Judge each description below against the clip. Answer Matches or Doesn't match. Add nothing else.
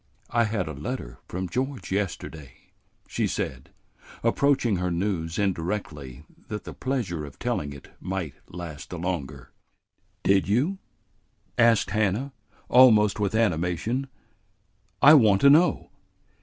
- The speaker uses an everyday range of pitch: Doesn't match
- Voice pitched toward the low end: Matches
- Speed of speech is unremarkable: Doesn't match